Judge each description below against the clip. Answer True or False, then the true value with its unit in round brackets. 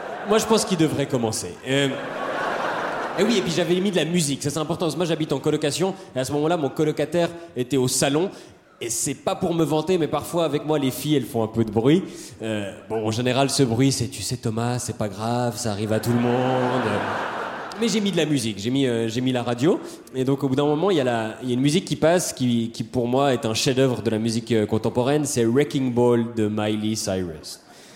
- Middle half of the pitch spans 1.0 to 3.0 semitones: False (4.8 semitones)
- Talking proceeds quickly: True (250 wpm)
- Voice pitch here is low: True (130 Hz)